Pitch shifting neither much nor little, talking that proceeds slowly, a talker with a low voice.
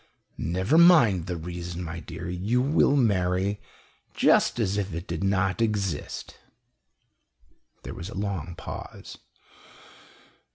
Yes: average, 3.3 semitones; slow, 120 wpm; very low, 95 Hz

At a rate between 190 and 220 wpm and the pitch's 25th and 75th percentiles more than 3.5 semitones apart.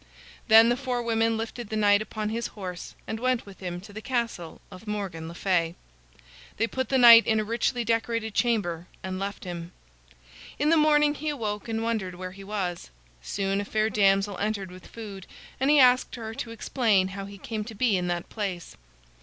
No: average, 200 wpm; average, 3.2 semitones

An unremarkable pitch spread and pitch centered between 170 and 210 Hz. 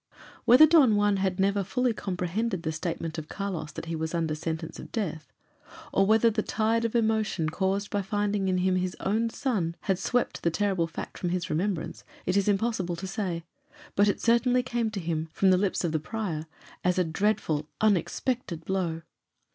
Yes: average, 4.4 semitones; high, 190 Hz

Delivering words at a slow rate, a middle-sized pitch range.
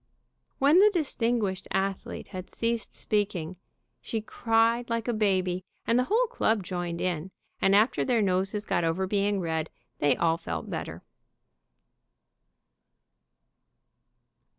Yes: slow, 125 wpm; average, 4.1 semitones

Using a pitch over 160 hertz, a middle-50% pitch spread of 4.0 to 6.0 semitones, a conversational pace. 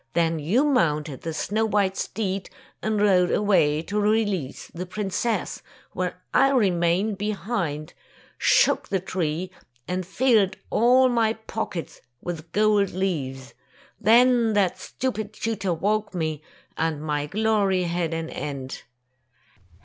No: high, 190 Hz; average, 4.8 semitones; slow, 125 wpm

